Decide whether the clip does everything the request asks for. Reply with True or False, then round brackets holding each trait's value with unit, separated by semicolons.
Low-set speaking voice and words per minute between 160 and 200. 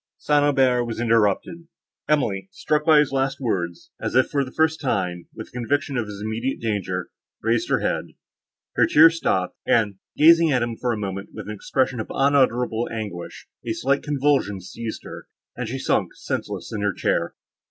True (120 Hz; 185 wpm)